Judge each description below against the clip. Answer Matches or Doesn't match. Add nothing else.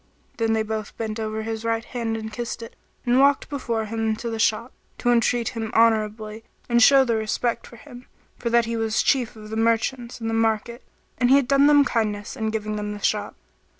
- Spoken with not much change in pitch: Matches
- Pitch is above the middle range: Matches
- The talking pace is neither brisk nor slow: Doesn't match